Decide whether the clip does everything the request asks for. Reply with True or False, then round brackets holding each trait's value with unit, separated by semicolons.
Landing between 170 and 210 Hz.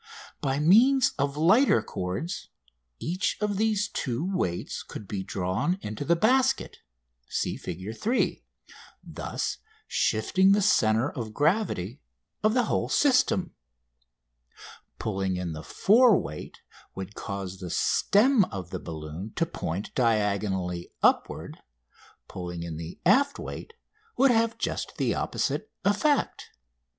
False (140 Hz)